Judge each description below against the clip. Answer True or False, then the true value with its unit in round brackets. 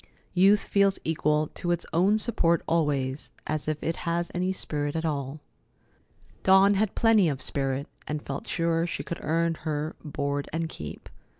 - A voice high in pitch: False (160 Hz)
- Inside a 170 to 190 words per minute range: False (160 wpm)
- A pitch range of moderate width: True (3.4 semitones)